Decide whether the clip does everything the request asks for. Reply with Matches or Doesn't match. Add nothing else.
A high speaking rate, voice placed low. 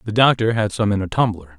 Matches